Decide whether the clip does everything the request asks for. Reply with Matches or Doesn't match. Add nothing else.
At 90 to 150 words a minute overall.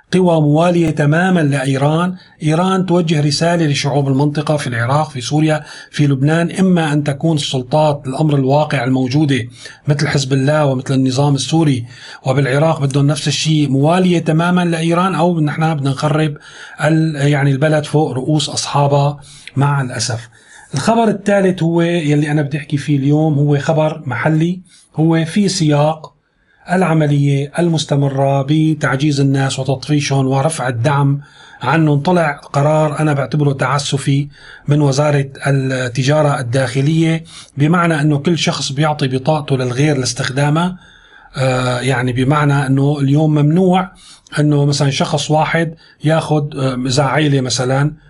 Matches